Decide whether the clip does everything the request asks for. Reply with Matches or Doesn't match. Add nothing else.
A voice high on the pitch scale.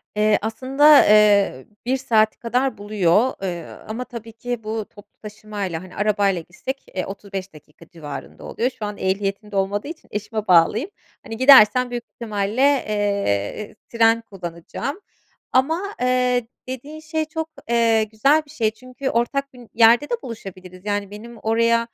Matches